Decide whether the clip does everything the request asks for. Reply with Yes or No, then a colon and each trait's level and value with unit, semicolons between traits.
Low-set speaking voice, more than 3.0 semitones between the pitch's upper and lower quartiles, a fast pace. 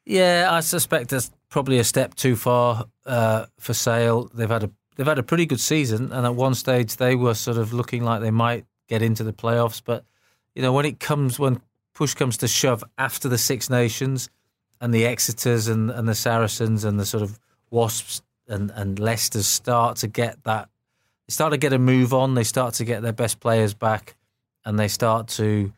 No: low, 120 Hz; narrow, 2.4 semitones; fast, 210 wpm